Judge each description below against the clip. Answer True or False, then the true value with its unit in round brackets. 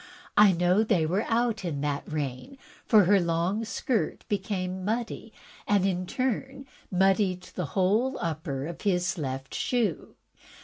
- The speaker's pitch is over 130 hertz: True (190 Hz)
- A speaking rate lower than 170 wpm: True (145 wpm)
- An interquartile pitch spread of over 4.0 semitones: True (4.4 semitones)